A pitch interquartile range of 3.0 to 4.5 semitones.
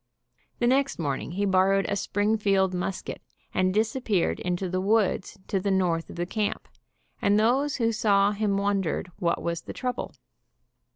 No: narrow, 2.6 semitones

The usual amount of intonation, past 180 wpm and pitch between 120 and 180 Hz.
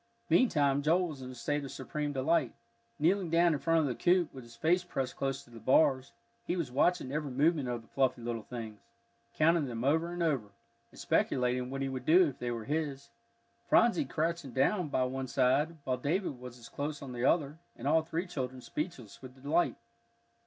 Yes: average, 4.3 semitones; fast, 205 wpm; medium, 140 Hz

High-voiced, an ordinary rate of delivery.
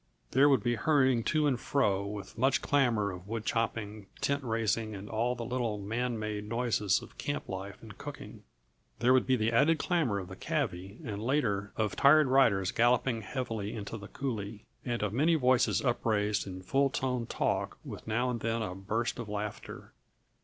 No: low, 115 Hz; average, 185 wpm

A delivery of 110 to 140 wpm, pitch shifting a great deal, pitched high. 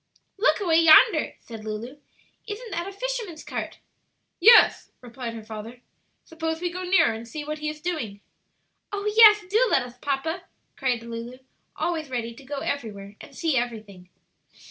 No: average, 165 wpm; wide, 7.3 semitones; very high, 295 Hz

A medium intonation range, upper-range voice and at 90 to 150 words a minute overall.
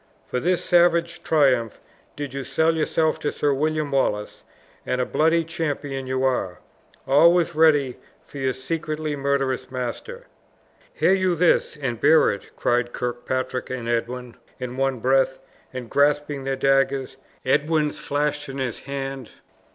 No: average, 3.2 semitones; low, 135 Hz; average, 145 wpm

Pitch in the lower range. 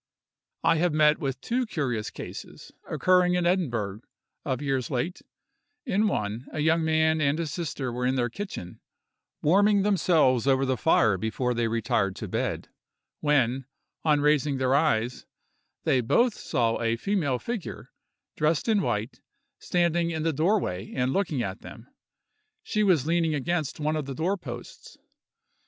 No: medium, 150 Hz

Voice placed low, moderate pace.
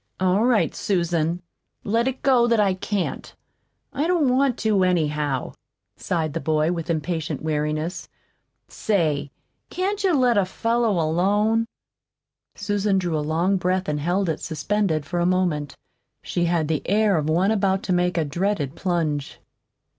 No: medium, 180 Hz; average, 155 wpm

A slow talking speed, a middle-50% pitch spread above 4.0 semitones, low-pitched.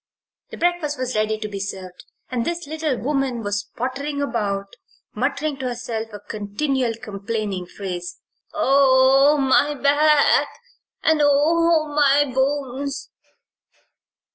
No: slow, 115 wpm; average, 5.2 semitones; very high, 265 Hz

